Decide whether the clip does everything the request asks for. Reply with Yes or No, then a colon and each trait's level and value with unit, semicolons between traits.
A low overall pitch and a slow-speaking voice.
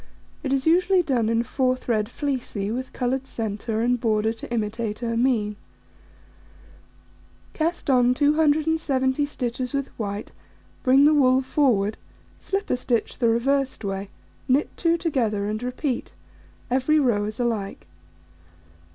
No: very high, 250 Hz; slow, 130 wpm